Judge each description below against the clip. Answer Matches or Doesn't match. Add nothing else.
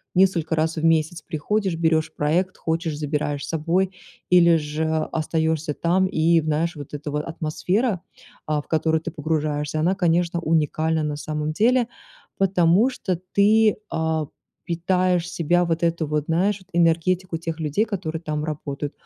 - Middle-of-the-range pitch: Matches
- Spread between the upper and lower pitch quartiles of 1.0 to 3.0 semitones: Matches